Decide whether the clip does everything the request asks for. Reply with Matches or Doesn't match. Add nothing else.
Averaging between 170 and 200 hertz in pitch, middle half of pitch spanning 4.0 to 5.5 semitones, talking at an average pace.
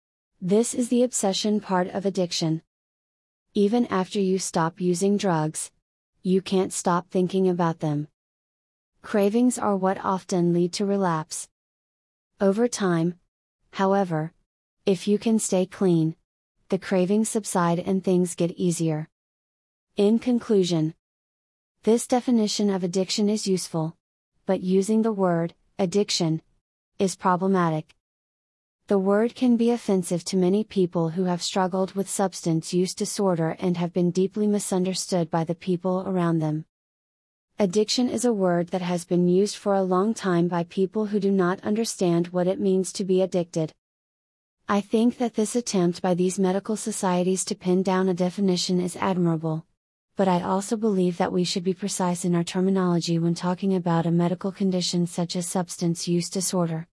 Doesn't match